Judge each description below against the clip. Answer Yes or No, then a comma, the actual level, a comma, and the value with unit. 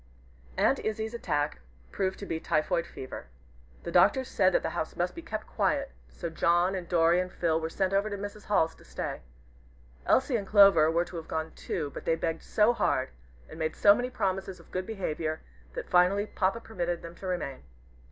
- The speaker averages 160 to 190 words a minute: No, average, 200 wpm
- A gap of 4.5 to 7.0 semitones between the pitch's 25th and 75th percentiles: No, average, 3.7 semitones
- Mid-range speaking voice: Yes, medium, 180 Hz